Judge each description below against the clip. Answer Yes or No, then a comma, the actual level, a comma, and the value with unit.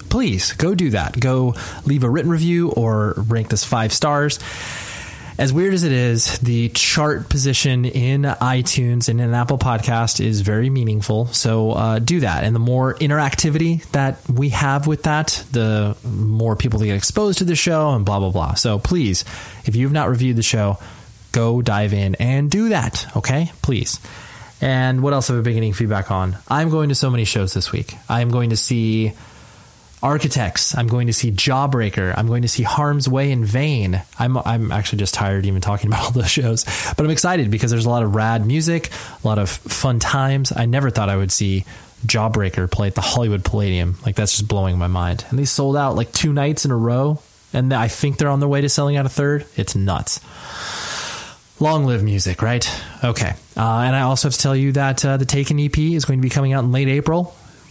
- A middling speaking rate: No, fast, 215 wpm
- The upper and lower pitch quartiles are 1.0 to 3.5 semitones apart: No, average, 4.3 semitones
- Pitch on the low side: Yes, low, 120 Hz